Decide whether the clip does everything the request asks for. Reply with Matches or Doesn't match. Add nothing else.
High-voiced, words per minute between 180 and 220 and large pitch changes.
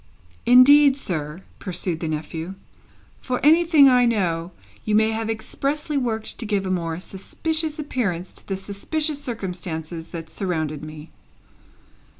Doesn't match